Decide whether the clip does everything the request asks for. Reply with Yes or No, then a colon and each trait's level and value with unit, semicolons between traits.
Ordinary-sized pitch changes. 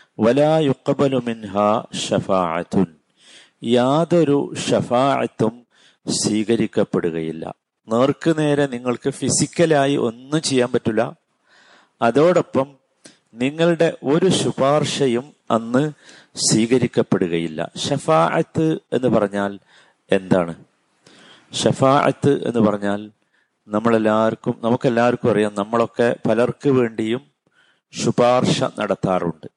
Yes: average, 4.3 semitones